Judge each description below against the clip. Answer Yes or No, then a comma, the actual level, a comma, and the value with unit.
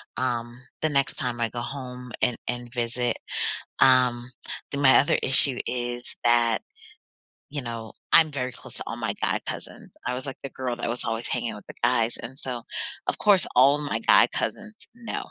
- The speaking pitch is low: Yes, low, 125 Hz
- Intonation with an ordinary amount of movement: No, narrow, 2.2 semitones